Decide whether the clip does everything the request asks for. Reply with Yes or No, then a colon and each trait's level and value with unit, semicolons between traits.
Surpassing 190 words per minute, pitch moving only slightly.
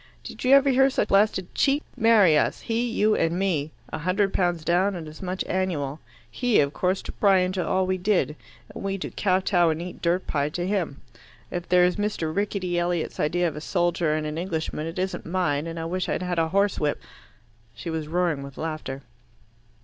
No: fast, 205 wpm; average, 3.3 semitones